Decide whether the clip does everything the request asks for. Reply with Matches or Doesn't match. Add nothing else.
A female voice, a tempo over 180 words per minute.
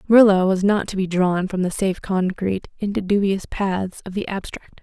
Matches